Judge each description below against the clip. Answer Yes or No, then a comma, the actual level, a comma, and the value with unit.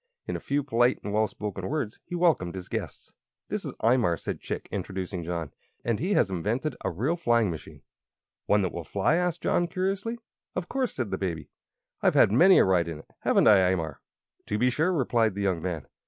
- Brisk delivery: Yes, fast, 210 wpm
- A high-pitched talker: No, low, 105 Hz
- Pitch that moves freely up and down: Yes, wide, 8.6 semitones